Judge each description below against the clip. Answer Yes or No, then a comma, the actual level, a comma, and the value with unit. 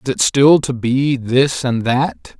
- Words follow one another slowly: No, average, 200 wpm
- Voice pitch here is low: Yes, low, 125 Hz